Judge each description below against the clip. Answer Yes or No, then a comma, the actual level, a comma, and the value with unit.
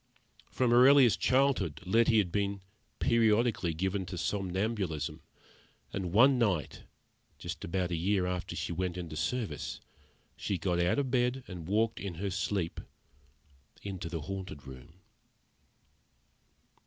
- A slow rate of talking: Yes, slow, 130 wpm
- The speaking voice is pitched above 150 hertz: No, very low, 95 Hz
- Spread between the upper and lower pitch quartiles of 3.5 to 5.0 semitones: Yes, average, 4.6 semitones